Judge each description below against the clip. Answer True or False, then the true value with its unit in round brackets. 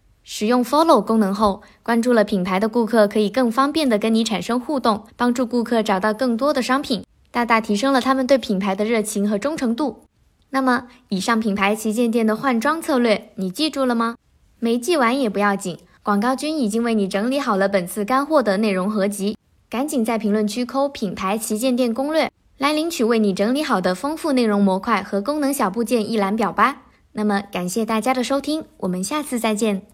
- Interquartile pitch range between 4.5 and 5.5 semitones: False (4.0 semitones)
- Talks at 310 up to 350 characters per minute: True (320 characters per minute)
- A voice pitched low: False (230 Hz)